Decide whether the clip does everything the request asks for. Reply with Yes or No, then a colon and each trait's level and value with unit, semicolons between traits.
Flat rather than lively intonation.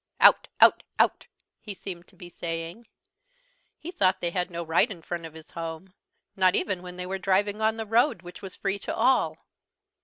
No: average, 3.0 semitones